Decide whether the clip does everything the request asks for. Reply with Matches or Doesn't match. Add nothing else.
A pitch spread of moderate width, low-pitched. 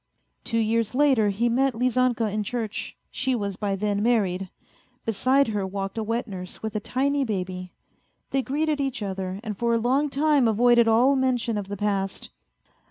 Doesn't match